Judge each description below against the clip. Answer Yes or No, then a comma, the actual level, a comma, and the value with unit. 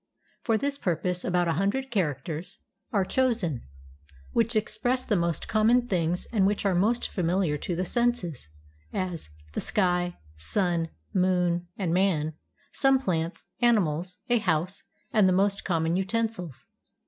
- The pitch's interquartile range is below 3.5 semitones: No, average, 4.2 semitones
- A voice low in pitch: No, medium, 185 Hz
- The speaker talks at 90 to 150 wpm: Yes, average, 145 wpm